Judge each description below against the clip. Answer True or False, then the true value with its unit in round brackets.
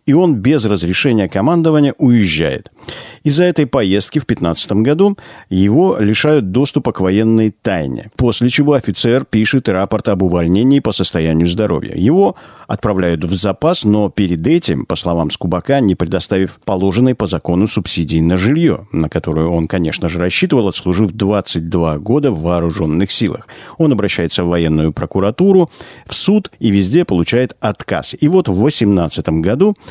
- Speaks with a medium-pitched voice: False (105 Hz)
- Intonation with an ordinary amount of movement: False (6.6 semitones)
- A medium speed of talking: True (150 wpm)